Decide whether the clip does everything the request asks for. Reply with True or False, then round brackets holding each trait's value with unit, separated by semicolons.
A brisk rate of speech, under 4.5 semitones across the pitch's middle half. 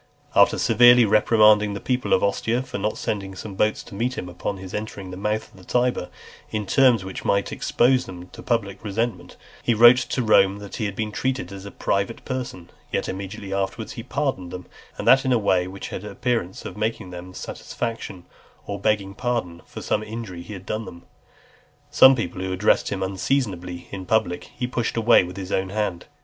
True (210 wpm; 3.4 semitones)